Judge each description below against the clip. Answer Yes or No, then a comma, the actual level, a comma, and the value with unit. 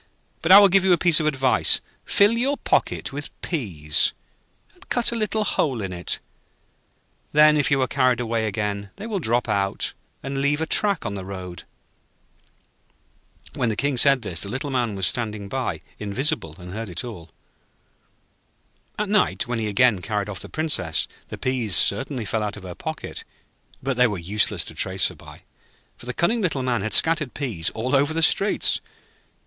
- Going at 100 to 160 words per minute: No, average, 185 wpm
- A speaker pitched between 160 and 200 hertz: No, low, 125 Hz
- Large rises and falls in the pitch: Yes, wide, 7.0 semitones